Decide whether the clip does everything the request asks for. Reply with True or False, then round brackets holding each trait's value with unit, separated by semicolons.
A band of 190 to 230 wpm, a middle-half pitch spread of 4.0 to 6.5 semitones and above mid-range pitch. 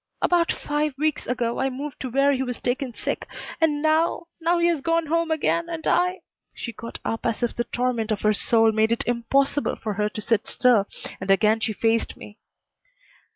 True (205 wpm; 5.6 semitones; 250 Hz)